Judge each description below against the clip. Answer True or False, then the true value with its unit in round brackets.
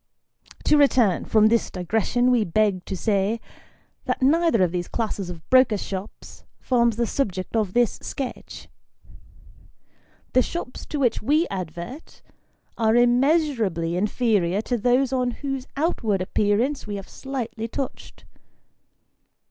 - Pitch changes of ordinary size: True (4.6 semitones)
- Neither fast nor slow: False (130 wpm)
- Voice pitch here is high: True (230 Hz)